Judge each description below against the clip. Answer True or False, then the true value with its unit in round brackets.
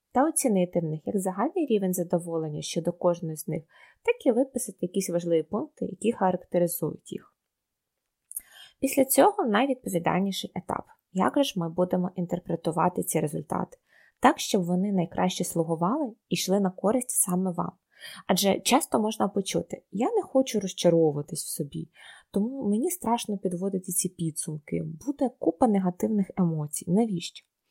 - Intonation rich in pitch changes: False (4.9 semitones)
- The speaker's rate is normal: True (140 wpm)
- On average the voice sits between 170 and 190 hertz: True (185 Hz)